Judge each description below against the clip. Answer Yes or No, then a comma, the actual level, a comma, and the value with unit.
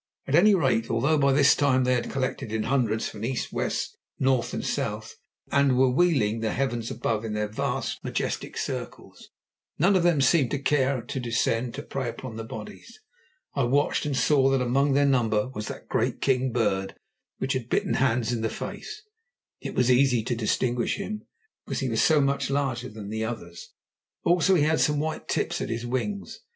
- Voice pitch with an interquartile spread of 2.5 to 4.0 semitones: Yes, average, 3.6 semitones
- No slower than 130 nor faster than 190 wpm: No, average, 200 wpm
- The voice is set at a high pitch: No, low, 130 Hz